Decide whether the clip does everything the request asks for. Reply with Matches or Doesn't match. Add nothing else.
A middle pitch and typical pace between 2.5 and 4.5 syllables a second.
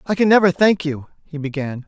Doesn't match